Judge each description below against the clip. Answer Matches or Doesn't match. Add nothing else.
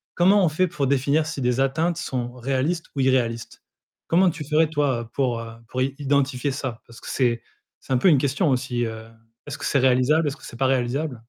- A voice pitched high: Doesn't match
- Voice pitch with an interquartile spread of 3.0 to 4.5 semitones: Matches